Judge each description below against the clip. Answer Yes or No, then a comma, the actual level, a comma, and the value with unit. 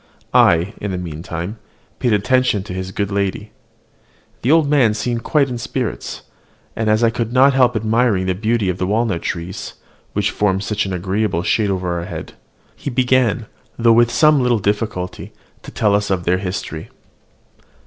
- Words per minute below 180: Yes, average, 170 wpm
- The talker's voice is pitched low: Yes, low, 105 Hz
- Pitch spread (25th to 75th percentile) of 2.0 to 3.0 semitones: No, average, 4.2 semitones